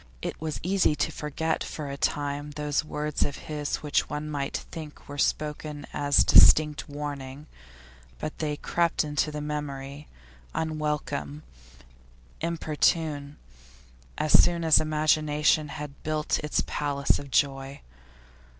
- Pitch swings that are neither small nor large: No, narrow, 1.2 semitones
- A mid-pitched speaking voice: Yes, medium, 150 Hz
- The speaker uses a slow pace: Yes, slow, 125 wpm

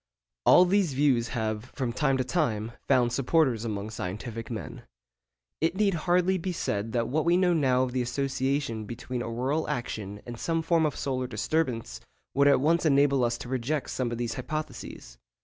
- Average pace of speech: Yes, average, 180 wpm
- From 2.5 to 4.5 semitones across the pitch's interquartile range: No, average, 4.9 semitones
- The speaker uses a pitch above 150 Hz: No, low, 130 Hz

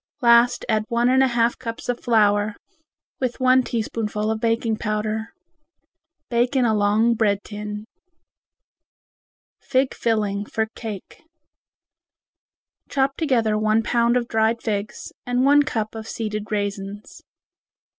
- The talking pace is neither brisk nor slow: No, slow, 125 wpm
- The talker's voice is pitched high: Yes, high, 225 Hz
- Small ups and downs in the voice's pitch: Yes, narrow, 2.3 semitones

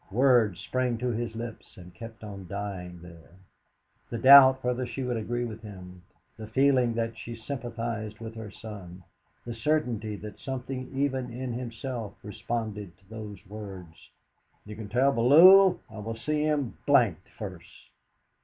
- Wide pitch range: No, average, 3.4 semitones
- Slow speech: No, average, 155 wpm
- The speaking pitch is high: No, low, 115 Hz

